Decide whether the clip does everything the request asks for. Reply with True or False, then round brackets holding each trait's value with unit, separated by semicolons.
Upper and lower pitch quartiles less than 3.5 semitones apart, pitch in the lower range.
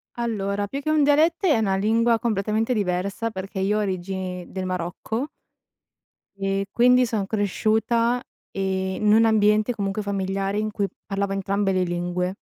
False (2.8 semitones; 200 Hz)